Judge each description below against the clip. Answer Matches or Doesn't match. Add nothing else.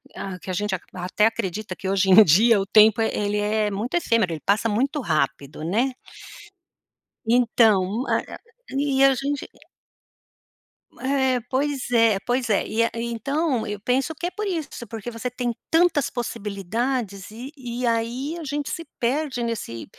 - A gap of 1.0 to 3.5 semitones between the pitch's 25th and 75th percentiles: Doesn't match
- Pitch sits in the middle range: Doesn't match